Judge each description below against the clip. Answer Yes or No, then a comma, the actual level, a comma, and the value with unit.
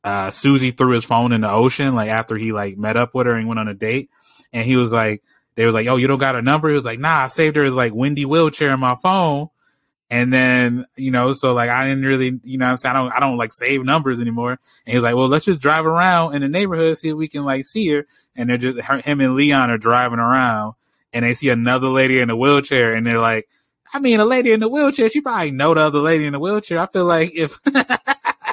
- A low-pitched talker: Yes, low, 130 Hz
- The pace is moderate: No, fast, 275 wpm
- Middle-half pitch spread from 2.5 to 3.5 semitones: No, average, 4.2 semitones